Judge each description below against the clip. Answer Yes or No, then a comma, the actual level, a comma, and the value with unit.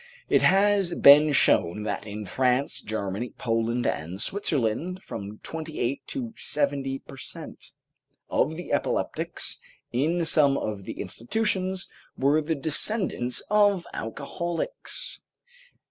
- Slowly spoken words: Yes, slow, 115 wpm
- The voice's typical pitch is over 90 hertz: Yes, medium, 140 Hz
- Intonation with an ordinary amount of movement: No, wide, 7.1 semitones